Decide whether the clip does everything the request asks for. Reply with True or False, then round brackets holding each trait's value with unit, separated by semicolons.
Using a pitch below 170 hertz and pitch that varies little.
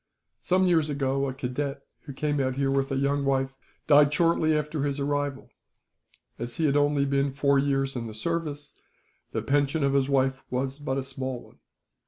True (140 Hz; 1.4 semitones)